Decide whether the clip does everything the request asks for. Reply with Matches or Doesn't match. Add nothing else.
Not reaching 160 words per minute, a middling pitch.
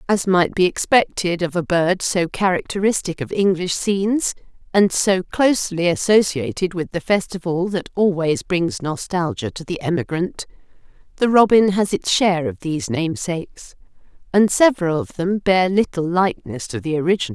Matches